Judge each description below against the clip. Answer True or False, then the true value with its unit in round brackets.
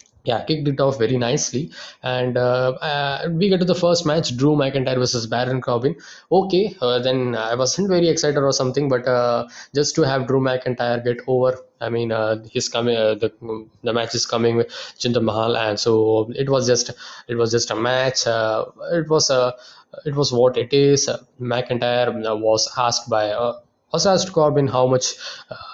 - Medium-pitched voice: False (125 Hz)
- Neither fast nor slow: True (185 wpm)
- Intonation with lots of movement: False (3.1 semitones)